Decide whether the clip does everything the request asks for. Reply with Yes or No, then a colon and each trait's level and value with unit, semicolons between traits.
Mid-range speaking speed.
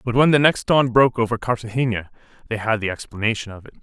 No: fast, 220 wpm